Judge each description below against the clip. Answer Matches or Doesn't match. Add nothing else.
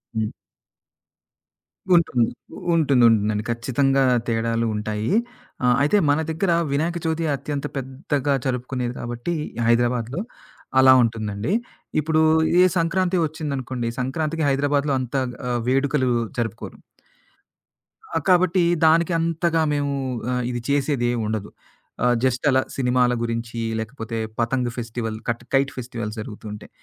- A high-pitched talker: Doesn't match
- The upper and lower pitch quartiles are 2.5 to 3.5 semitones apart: Doesn't match